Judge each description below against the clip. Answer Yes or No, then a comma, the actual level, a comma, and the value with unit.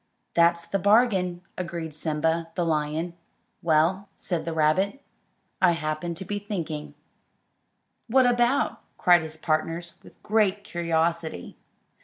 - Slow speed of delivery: Yes, slow, 120 wpm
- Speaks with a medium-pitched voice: Yes, medium, 170 Hz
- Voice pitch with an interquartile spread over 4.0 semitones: No, average, 3.3 semitones